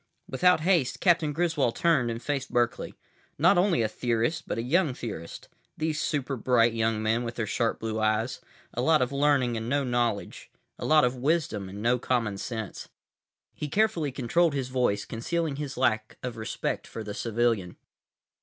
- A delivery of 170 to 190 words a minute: Yes, average, 180 wpm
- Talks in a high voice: No, low, 125 Hz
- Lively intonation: No, average, 4.7 semitones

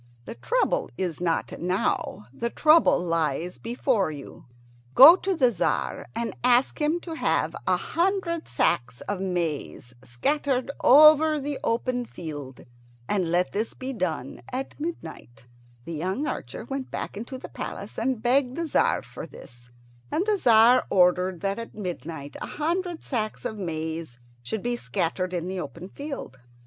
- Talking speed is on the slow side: No, average, 155 wpm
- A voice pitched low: No, high, 220 Hz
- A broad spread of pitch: Yes, wide, 8.7 semitones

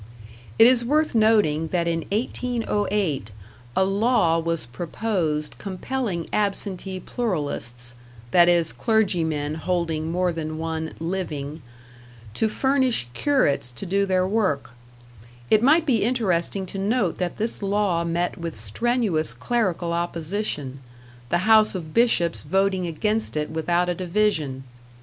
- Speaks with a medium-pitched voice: Yes, medium, 180 Hz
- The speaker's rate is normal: No, slow, 125 wpm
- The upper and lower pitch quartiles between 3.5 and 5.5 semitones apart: Yes, average, 5.0 semitones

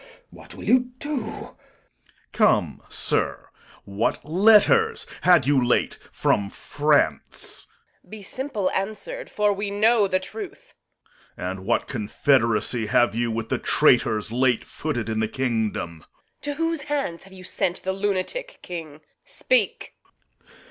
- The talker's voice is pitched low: No, medium, 175 Hz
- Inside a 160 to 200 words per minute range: No, average, 140 wpm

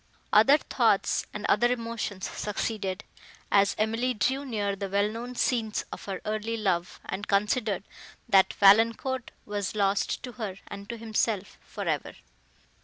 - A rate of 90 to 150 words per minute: Yes, average, 145 wpm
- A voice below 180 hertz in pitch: No, high, 215 Hz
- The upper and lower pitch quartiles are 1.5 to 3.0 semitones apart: Yes, narrow, 2.5 semitones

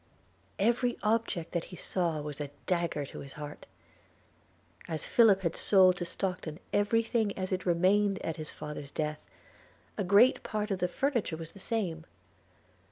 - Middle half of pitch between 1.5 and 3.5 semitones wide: No, average, 4.3 semitones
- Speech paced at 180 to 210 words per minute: No, average, 165 wpm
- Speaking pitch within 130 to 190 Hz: Yes, medium, 185 Hz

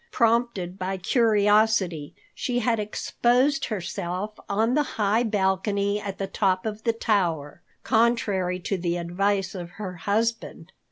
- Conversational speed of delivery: No, slow, 130 wpm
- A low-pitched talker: No, high, 205 Hz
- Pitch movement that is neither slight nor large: Yes, average, 3.4 semitones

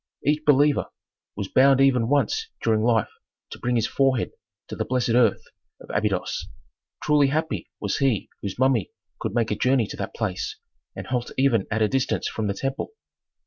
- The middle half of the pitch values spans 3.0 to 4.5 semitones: Yes, average, 3.7 semitones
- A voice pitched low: Yes, low, 125 Hz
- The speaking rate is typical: Yes, average, 180 wpm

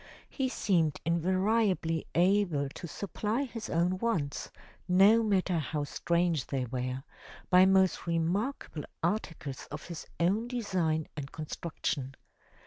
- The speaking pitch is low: No, medium, 175 Hz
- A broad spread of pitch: No, average, 4.5 semitones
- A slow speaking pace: Yes, slow, 120 wpm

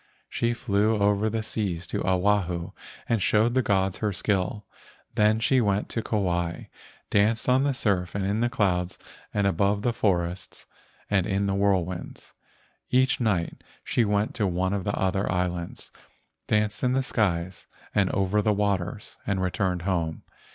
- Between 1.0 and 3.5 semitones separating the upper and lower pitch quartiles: Yes, average, 2.7 semitones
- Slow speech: No, average, 160 wpm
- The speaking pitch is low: Yes, low, 100 Hz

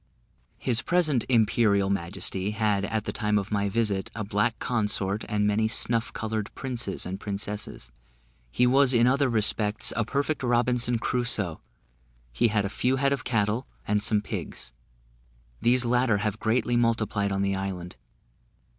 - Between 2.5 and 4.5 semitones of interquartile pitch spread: Yes, average, 3.2 semitones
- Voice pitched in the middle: No, low, 110 Hz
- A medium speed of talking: Yes, average, 155 wpm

